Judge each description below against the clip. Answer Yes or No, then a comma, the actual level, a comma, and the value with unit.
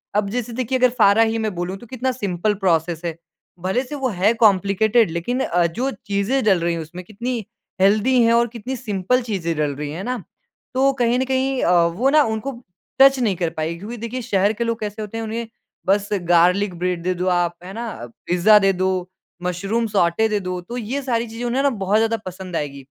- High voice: Yes, high, 210 Hz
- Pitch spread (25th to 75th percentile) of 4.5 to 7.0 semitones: Yes, average, 4.9 semitones